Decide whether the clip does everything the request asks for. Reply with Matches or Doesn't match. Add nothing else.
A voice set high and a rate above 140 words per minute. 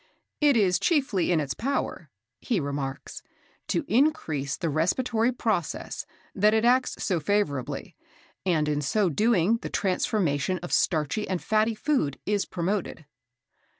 Doesn't match